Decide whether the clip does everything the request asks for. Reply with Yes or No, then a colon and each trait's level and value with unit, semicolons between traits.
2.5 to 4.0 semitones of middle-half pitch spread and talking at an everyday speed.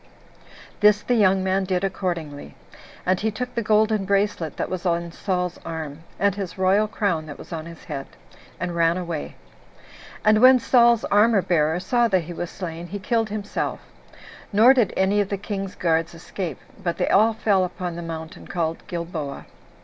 Yes: average, 3.6 semitones; average, 180 wpm